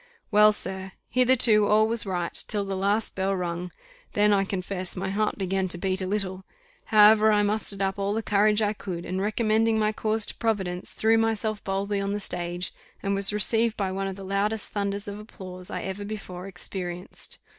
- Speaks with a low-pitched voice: No, high, 200 Hz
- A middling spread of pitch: No, narrow, 2.0 semitones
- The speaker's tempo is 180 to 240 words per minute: Yes, average, 195 wpm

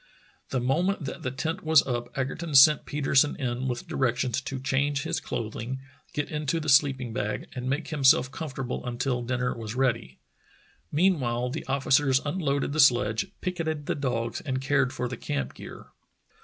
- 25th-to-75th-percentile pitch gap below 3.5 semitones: Yes, average, 2.9 semitones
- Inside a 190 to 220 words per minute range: No, average, 170 wpm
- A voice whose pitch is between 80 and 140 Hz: Yes, low, 135 Hz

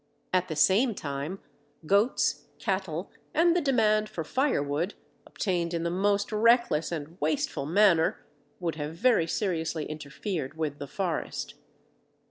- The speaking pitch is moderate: Yes, medium, 175 Hz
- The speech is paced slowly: Yes, slow, 130 wpm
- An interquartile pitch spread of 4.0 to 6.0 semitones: Yes, average, 5.2 semitones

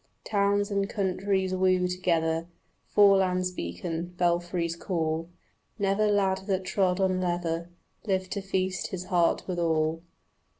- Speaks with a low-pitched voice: No, medium, 185 Hz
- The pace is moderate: No, slow, 125 wpm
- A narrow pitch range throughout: Yes, narrow, 2.1 semitones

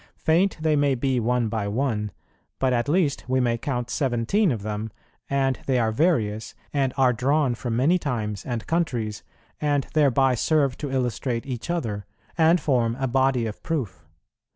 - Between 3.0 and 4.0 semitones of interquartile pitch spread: Yes, average, 3.7 semitones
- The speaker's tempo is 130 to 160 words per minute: No, average, 170 wpm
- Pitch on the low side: Yes, low, 130 Hz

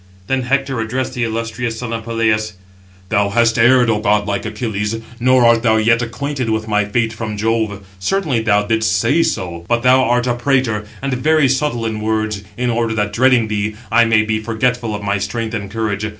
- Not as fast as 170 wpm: No, average, 195 wpm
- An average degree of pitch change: No, narrow, 2.3 semitones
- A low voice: Yes, low, 115 Hz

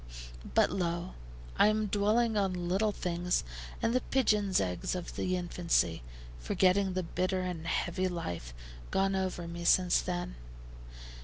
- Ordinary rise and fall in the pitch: No, narrow, 2.3 semitones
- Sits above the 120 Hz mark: Yes, medium, 185 Hz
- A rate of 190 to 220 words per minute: No, average, 140 wpm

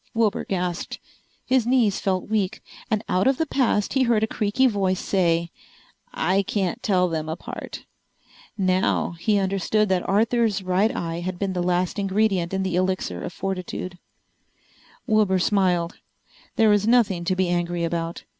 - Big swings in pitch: No, average, 3.2 semitones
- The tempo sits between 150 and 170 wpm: Yes, average, 160 wpm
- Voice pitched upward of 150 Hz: Yes, high, 190 Hz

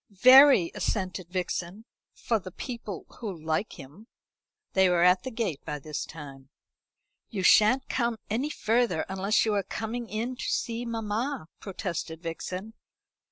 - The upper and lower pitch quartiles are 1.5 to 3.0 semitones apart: No, average, 4.7 semitones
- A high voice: Yes, high, 200 Hz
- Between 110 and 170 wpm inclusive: Yes, average, 145 wpm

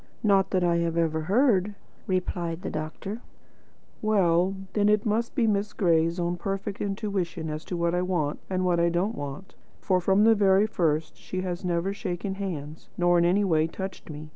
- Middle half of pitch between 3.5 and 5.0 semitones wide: No, average, 2.9 semitones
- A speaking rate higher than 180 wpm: Yes, average, 190 wpm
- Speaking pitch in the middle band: Yes, medium, 180 Hz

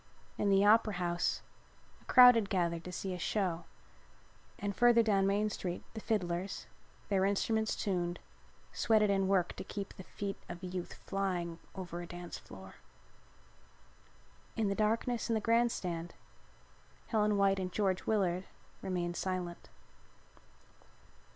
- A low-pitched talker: No, high, 195 Hz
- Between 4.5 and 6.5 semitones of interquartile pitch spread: No, average, 3.0 semitones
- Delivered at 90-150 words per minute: Yes, average, 140 wpm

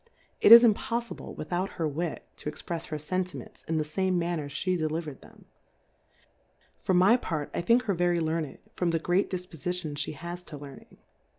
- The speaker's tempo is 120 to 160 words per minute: No, average, 190 wpm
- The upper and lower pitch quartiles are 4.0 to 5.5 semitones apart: No, average, 2.9 semitones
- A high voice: No, medium, 170 Hz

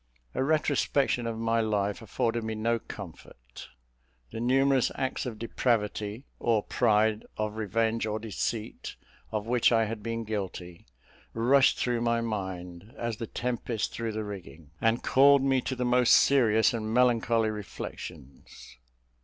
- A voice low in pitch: Yes, low, 115 Hz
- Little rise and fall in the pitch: Yes, narrow, 2.2 semitones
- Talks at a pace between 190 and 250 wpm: No, average, 145 wpm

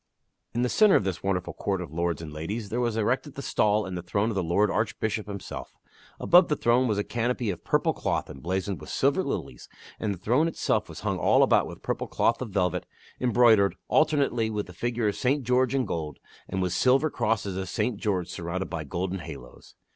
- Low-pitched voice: Yes, low, 105 Hz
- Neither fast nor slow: No, fast, 215 wpm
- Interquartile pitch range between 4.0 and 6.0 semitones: Yes, average, 4.9 semitones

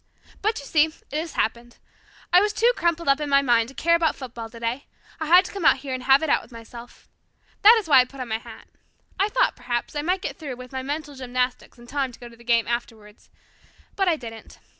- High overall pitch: Yes, very high, 270 Hz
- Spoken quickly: Yes, fast, 245 wpm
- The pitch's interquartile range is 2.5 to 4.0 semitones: No, average, 5.0 semitones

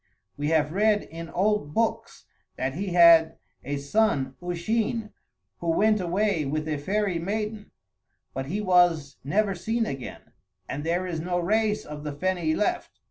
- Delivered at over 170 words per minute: No, average, 155 wpm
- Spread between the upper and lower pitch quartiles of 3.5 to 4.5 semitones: No, average, 5.3 semitones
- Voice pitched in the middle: Yes, medium, 175 Hz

